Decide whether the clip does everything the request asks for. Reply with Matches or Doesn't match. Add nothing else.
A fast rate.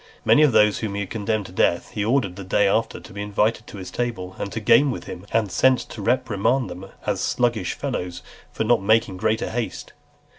Matches